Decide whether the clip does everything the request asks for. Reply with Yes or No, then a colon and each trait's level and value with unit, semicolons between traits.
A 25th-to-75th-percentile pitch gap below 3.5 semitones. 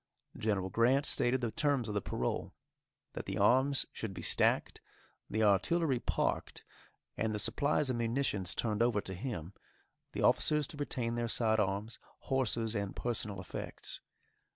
No: average, 4.2 semitones